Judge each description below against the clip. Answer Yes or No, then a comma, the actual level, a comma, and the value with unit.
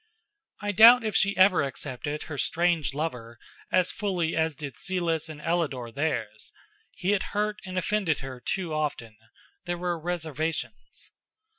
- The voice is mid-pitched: Yes, medium, 165 Hz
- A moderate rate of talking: Yes, average, 145 wpm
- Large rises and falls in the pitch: No, average, 4.1 semitones